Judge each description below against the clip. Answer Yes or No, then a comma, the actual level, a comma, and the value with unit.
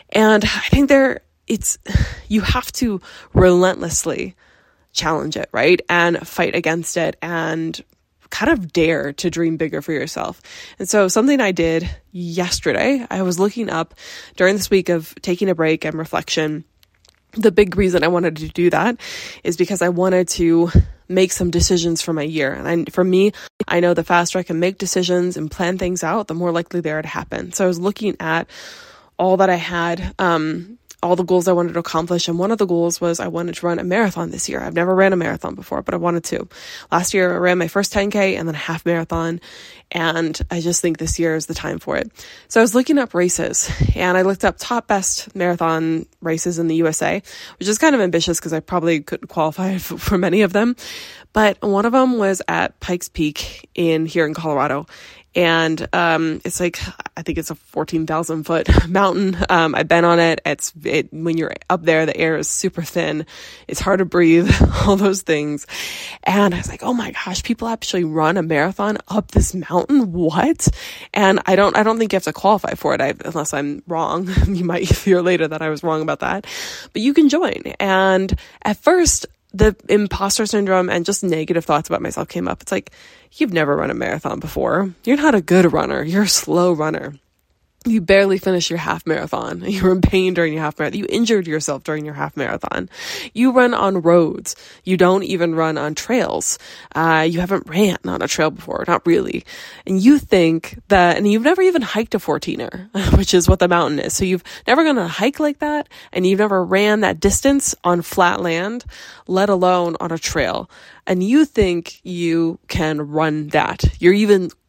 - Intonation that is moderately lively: Yes, average, 3.2 semitones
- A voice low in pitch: No, medium, 180 Hz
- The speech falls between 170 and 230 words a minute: Yes, fast, 205 wpm